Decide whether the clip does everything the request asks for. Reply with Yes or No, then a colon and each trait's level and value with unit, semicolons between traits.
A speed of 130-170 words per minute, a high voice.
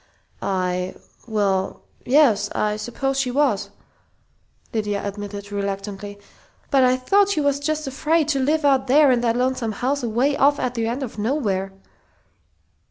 Yes: average, 150 wpm; high, 245 Hz